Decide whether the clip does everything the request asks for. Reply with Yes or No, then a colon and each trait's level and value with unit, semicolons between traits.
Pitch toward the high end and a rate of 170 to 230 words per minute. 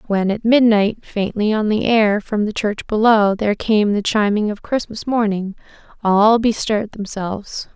No: high, 210 Hz; average, 160 wpm